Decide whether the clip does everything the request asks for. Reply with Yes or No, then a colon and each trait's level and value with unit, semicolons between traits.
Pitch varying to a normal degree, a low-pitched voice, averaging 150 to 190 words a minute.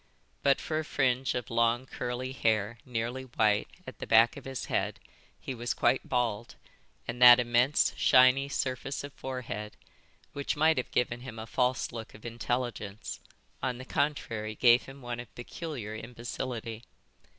No: narrow, 2.3 semitones; low, 120 Hz; average, 160 wpm